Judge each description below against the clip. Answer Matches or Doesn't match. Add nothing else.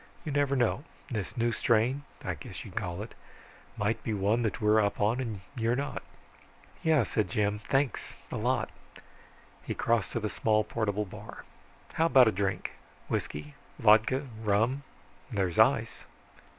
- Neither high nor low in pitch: Doesn't match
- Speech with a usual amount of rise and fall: Matches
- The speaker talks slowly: Doesn't match